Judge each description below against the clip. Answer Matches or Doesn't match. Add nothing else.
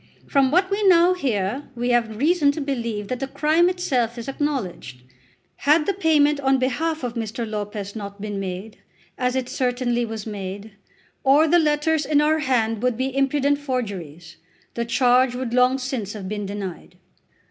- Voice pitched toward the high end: Matches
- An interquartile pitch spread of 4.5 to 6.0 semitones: Matches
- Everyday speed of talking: Matches